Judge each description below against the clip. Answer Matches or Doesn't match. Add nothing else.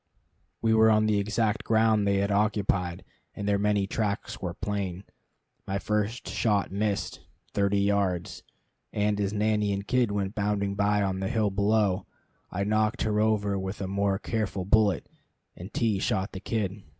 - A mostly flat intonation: Matches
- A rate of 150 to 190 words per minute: Matches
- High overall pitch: Doesn't match